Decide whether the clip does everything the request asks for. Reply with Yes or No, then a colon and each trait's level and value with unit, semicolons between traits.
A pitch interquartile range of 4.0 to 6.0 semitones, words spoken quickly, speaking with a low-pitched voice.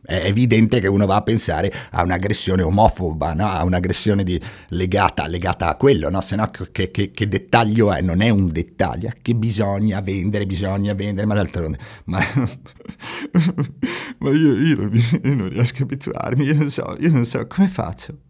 Yes: average, 4.4 semitones; fast, 175 wpm; low, 105 Hz